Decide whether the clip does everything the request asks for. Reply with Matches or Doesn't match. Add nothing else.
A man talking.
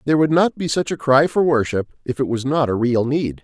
Matches